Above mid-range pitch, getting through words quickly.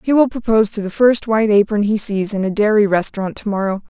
Yes: high, 210 Hz; fast, 240 wpm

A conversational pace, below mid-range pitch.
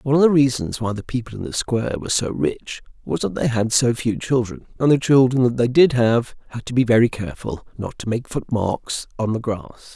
No: fast, 240 wpm; low, 120 Hz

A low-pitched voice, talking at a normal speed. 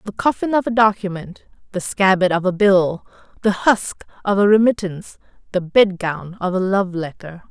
No: high, 190 Hz; average, 175 wpm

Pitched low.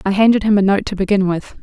No: high, 200 Hz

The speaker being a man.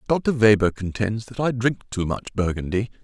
Yes: male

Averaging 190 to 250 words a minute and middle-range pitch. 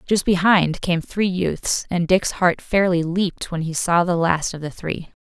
Yes: fast, 205 wpm; medium, 175 Hz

